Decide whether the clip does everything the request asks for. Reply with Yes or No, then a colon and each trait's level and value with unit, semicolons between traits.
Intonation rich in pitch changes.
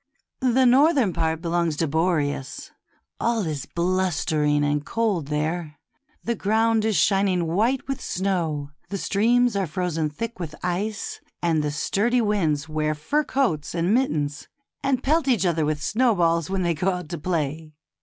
Yes: wide, 6.1 semitones